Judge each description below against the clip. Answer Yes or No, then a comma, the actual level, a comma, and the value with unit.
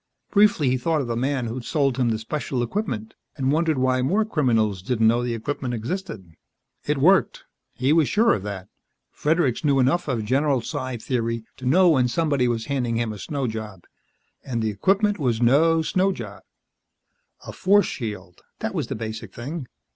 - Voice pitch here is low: Yes, low, 130 Hz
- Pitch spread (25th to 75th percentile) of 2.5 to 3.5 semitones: No, average, 5.1 semitones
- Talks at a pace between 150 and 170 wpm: No, average, 185 wpm